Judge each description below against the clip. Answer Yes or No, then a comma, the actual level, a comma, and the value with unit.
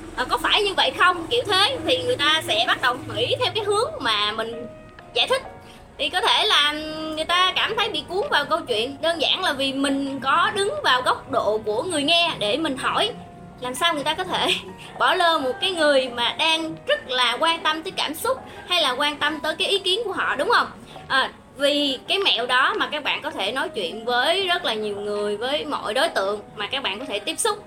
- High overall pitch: Yes, very high, 315 Hz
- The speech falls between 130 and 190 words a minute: No, average, 240 wpm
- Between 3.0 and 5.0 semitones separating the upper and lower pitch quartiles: No, wide, 5.5 semitones